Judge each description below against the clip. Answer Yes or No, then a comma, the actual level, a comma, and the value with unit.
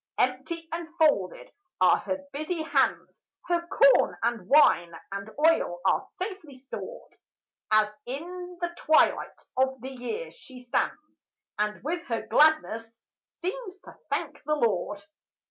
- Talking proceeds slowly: Yes, slow, 130 wpm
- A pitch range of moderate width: No, wide, 6.4 semitones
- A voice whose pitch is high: Yes, very high, 285 Hz